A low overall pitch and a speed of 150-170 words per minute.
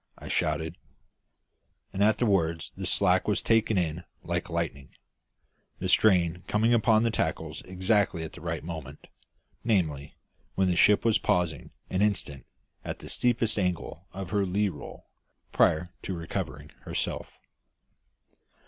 No: very low, 90 Hz; average, 140 wpm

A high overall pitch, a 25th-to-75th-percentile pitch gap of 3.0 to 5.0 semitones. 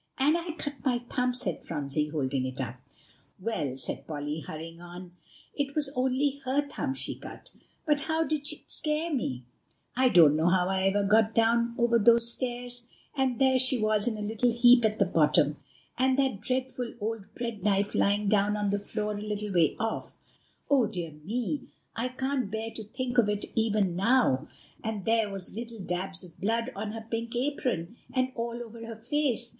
Yes: high, 225 Hz; average, 4.5 semitones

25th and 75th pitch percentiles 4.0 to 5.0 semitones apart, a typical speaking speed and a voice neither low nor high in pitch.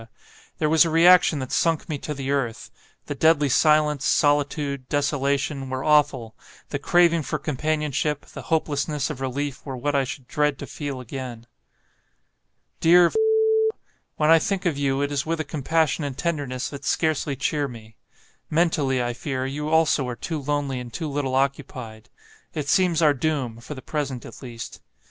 No: narrow, 2.6 semitones; average, 170 wpm; medium, 145 Hz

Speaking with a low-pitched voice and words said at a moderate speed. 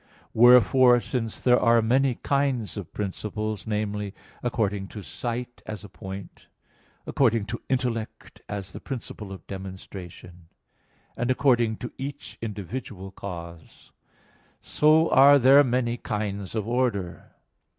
No: low, 110 Hz; slow, 120 wpm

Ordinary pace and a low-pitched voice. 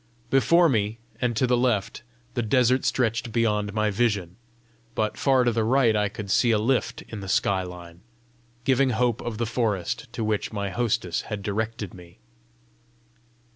Yes: average, 170 wpm; low, 110 Hz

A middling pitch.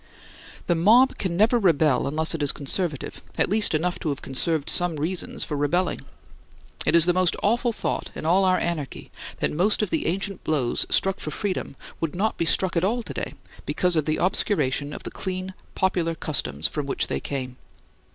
Yes: medium, 170 Hz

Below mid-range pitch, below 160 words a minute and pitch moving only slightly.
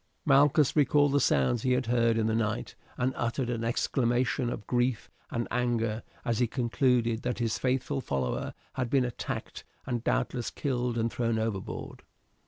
No: low, 120 Hz; average, 165 wpm; narrow, 1.9 semitones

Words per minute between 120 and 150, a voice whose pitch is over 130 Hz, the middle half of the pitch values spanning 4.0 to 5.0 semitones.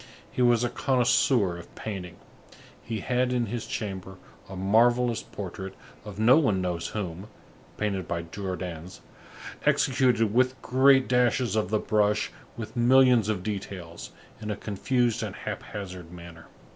No: average, 145 wpm; low, 105 Hz; average, 4.5 semitones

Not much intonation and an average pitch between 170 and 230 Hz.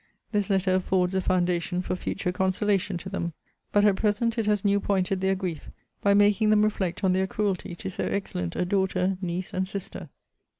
Yes: narrow, 1.9 semitones; high, 190 Hz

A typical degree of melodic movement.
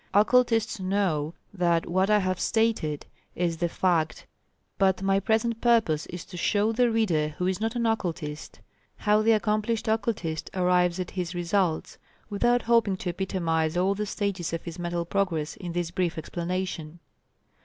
Yes: average, 3.8 semitones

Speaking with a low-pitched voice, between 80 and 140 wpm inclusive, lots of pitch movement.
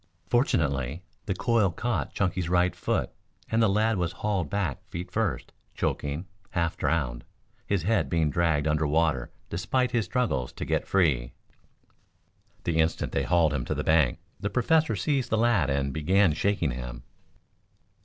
No: very low, 85 Hz; average, 155 wpm; wide, 5.7 semitones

